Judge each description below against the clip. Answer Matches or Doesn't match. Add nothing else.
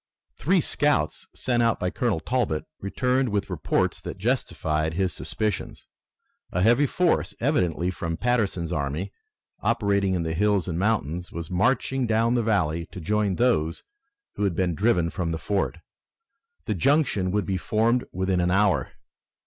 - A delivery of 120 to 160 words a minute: Matches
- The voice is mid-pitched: Doesn't match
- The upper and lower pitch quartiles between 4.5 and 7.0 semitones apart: Matches